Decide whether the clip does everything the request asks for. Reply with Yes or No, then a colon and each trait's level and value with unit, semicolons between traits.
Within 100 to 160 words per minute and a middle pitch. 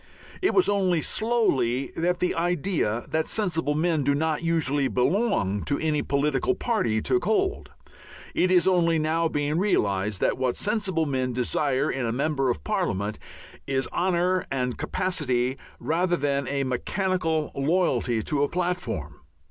Yes: average, 150 wpm; medium, 155 Hz